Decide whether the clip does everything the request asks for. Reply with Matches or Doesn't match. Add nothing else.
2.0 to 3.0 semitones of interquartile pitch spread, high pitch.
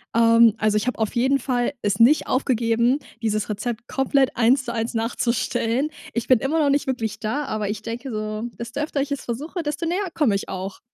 Doesn't match